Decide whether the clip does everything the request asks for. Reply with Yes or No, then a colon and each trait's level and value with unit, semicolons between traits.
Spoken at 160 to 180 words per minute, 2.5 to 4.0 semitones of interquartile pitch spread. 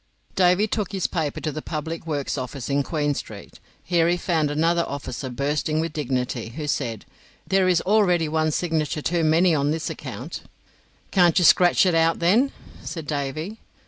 Yes: average, 175 wpm; average, 3.3 semitones